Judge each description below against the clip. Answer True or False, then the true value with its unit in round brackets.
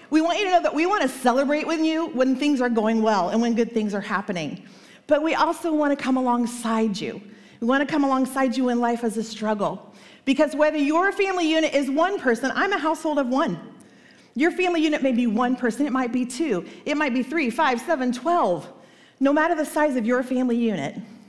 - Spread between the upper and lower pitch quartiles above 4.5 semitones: True (5.0 semitones)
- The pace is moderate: False (230 wpm)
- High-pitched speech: True (265 Hz)